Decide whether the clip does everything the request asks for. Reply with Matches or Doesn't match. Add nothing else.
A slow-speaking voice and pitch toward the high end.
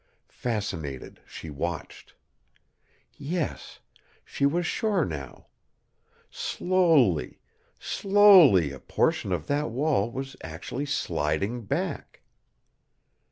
Doesn't match